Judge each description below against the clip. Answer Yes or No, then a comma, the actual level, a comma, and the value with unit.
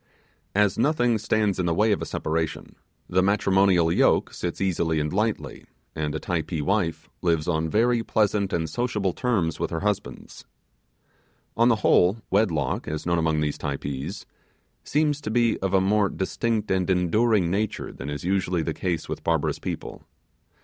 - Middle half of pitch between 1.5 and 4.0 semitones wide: No, average, 4.6 semitones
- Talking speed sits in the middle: Yes, average, 165 wpm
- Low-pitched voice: Yes, very low, 95 Hz